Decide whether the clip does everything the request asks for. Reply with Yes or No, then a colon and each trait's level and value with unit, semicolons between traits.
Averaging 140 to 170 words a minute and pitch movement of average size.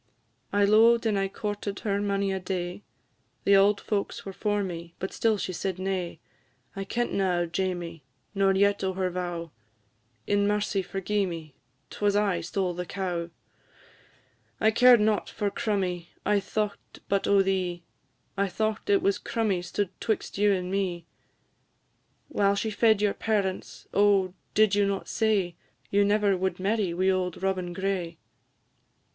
No: average, 155 wpm; narrow, 2.2 semitones